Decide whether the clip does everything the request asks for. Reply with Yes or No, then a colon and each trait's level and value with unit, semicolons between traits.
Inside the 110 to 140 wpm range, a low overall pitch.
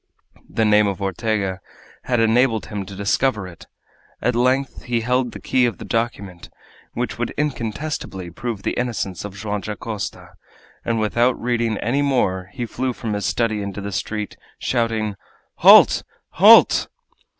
No: average, 150 wpm; low, 110 Hz